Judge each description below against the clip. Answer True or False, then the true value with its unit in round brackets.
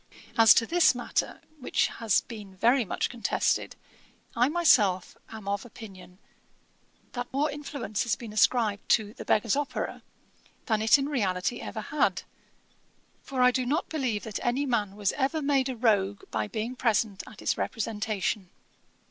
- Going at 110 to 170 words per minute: True (155 wpm)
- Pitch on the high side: True (230 Hz)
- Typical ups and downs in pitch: True (4.0 semitones)